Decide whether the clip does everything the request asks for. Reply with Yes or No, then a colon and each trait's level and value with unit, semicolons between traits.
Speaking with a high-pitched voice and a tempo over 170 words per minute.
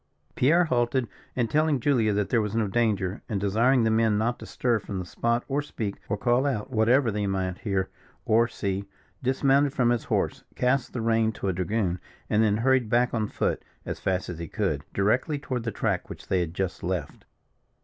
No: low, 115 Hz; fast, 205 wpm